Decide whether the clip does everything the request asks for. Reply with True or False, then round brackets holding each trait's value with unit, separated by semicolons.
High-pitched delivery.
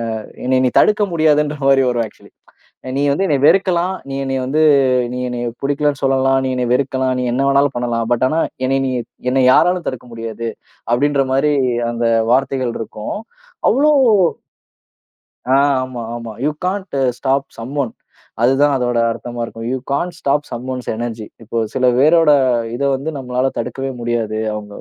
False (130 Hz)